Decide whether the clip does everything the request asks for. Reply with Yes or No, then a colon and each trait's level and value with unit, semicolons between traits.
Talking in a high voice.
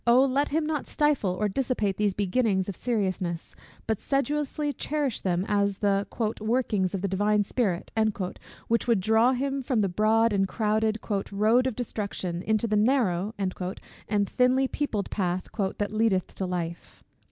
Yes: high, 215 Hz